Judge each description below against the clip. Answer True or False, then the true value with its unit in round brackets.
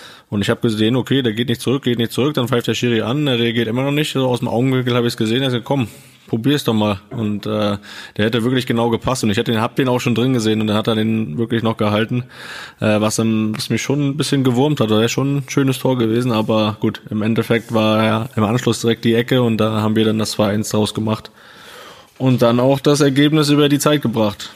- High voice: False (115 Hz)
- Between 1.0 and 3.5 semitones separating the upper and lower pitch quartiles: True (2.8 semitones)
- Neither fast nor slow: False (260 wpm)